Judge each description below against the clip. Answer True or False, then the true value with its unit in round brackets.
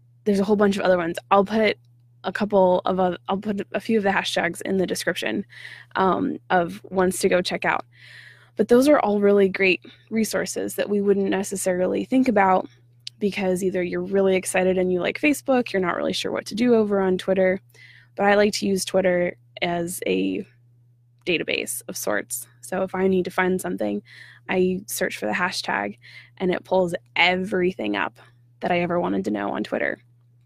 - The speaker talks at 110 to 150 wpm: False (195 wpm)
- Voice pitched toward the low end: False (185 Hz)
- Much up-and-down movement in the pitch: True (8.2 semitones)